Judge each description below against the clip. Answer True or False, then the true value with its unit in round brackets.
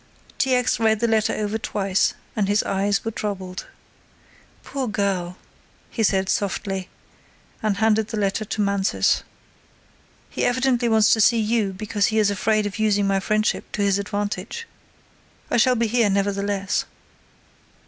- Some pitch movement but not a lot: False (1.9 semitones)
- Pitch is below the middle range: False (210 Hz)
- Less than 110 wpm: False (150 wpm)